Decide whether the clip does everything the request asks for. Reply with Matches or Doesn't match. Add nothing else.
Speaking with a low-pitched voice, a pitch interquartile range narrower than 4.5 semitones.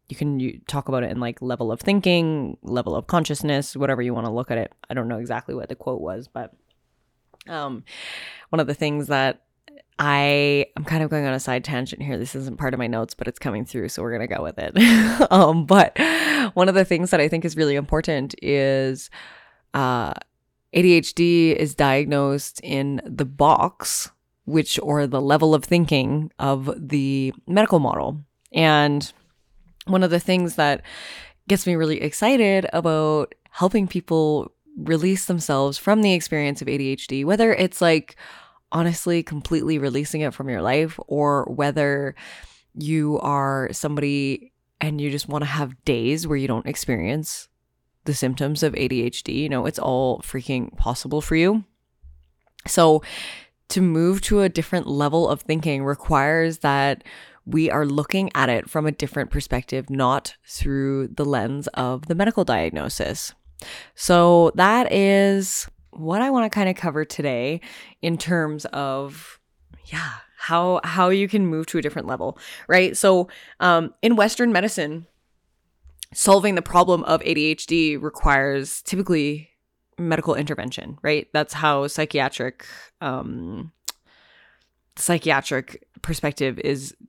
Doesn't match